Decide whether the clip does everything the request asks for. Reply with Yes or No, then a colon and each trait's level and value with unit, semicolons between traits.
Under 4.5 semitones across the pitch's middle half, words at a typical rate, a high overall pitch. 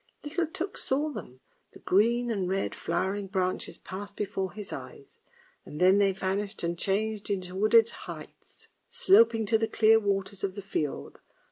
Yes: average, 2.9 semitones; average, 165 wpm; high, 200 Hz